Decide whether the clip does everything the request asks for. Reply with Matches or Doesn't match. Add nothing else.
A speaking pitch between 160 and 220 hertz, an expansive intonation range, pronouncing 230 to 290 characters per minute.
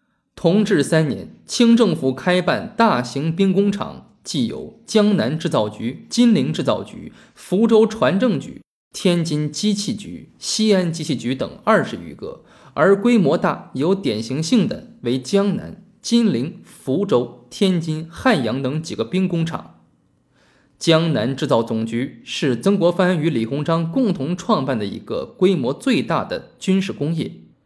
Doesn't match